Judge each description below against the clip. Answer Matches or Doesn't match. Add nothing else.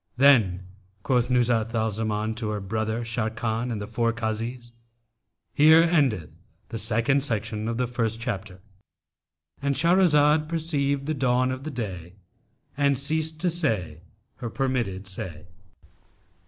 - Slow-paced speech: Matches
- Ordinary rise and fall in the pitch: Matches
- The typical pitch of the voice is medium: Doesn't match